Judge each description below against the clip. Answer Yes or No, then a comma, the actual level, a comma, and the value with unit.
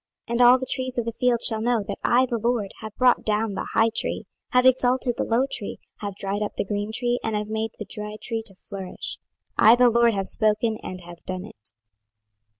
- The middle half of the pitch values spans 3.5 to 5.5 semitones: No, average, 2.9 semitones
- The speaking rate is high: Yes, fast, 230 wpm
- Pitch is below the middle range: No, high, 225 Hz